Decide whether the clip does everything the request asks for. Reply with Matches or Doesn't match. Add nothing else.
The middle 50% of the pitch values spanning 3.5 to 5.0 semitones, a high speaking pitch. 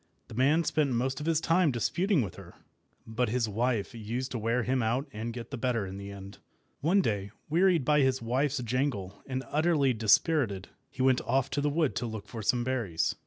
Doesn't match